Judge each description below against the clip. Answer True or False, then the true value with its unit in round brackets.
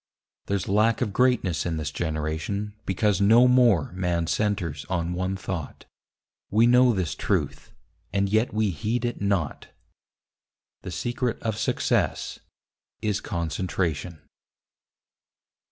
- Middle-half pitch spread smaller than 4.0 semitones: False (4.3 semitones)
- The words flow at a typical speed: False (120 wpm)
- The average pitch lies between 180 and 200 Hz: False (100 Hz)